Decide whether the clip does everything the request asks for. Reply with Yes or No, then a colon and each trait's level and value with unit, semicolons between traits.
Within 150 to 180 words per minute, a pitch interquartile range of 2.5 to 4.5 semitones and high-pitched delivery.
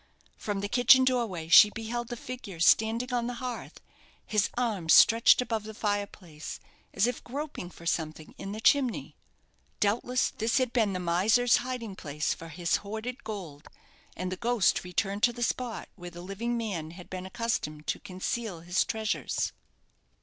No: average, 165 wpm; average, 4.9 semitones; high, 215 Hz